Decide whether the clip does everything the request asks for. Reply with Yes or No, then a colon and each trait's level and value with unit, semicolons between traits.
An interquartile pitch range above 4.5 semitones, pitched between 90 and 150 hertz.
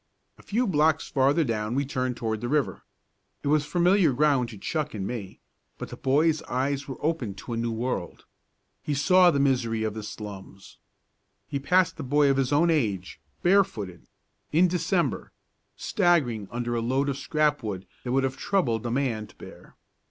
Yes: average, 5.1 semitones; low, 135 Hz